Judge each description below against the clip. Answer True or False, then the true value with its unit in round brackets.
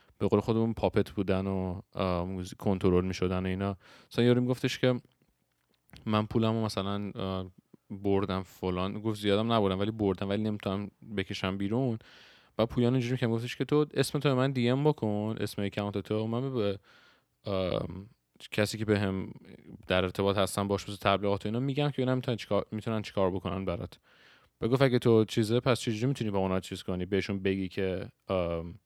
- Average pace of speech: False (160 wpm)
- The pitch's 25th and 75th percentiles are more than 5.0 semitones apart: False (3.3 semitones)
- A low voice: True (100 Hz)